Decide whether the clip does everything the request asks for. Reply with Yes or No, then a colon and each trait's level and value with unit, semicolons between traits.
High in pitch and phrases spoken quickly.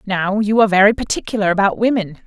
No: high, 200 Hz; average, 185 wpm